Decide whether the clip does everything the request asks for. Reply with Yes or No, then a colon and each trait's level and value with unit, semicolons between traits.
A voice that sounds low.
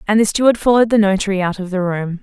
No: high, 200 Hz